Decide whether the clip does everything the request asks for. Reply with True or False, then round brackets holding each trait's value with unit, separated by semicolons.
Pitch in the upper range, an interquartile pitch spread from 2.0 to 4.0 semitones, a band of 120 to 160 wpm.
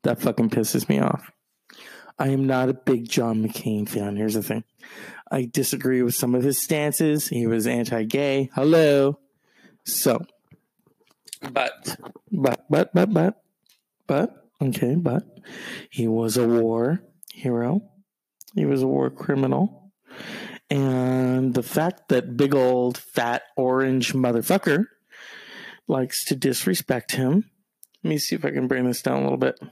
False (130 Hz; 3.7 semitones; 145 wpm)